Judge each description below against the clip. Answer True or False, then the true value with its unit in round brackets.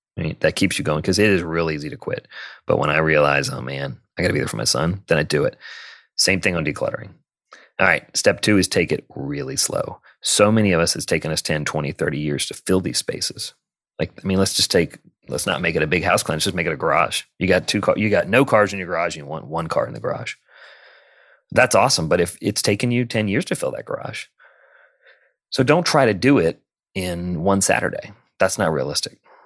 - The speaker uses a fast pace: True (250 wpm)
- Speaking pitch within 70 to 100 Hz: True (95 Hz)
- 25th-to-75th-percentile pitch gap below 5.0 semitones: False (5.5 semitones)